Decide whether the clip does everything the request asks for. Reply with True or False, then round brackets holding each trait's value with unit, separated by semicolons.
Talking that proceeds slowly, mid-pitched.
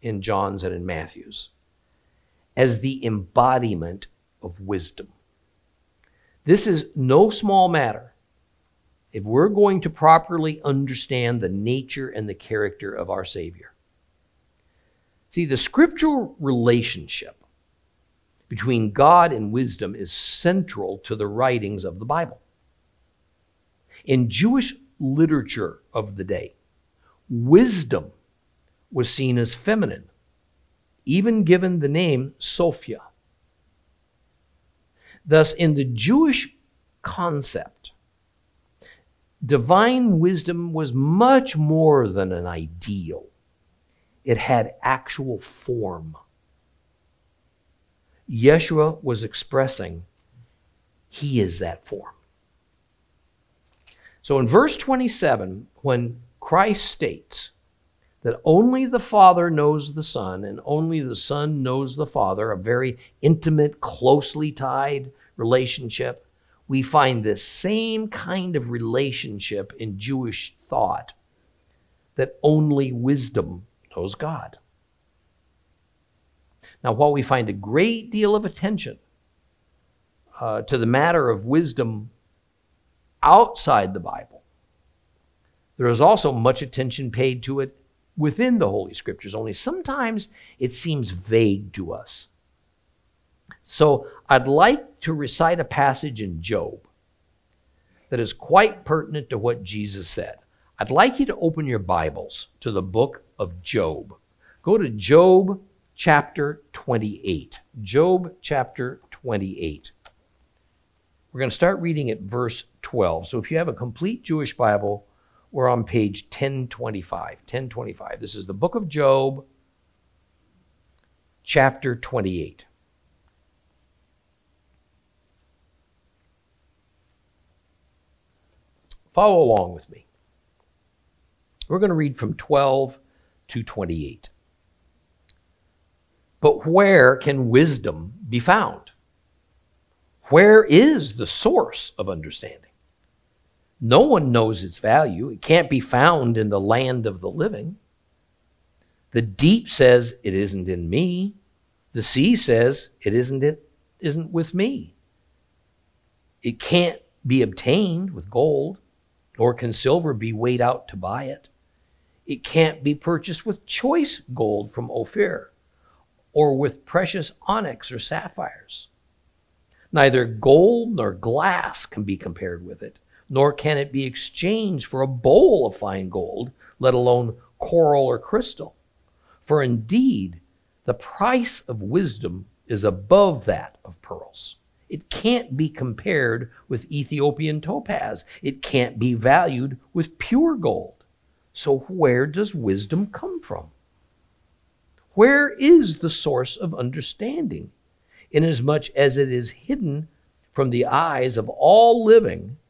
False (115 wpm; 125 Hz)